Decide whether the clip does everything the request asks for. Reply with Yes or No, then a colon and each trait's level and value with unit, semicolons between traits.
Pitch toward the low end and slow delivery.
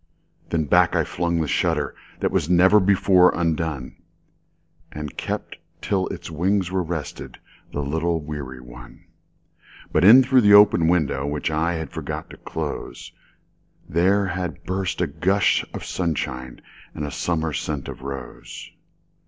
Yes: very low, 85 Hz; slow, 130 wpm